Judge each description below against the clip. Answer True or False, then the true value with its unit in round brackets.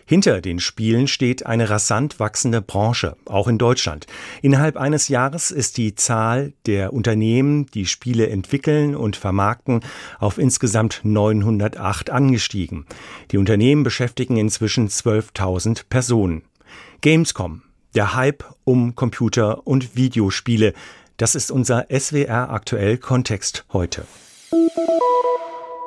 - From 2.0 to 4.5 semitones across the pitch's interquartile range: True (4.0 semitones)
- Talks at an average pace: False (110 wpm)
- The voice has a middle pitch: False (115 Hz)